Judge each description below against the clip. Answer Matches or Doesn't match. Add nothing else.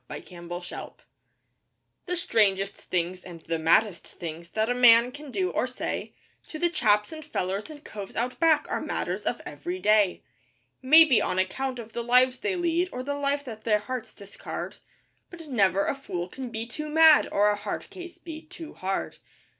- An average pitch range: Doesn't match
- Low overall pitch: Doesn't match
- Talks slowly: Doesn't match